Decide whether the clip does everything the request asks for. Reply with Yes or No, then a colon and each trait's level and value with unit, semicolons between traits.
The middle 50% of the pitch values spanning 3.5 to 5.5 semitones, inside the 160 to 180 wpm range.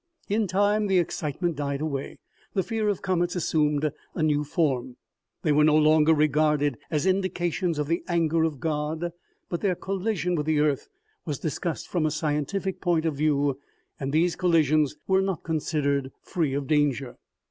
No: average, 3.1 semitones; average, 170 wpm